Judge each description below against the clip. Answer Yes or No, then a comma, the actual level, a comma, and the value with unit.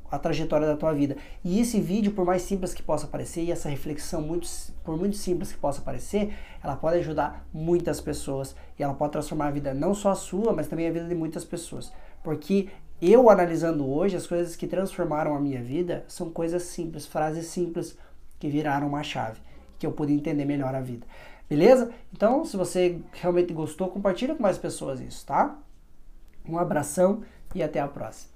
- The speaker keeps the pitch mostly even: No, average, 3.3 semitones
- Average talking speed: No, fast, 195 wpm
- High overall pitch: No, medium, 165 Hz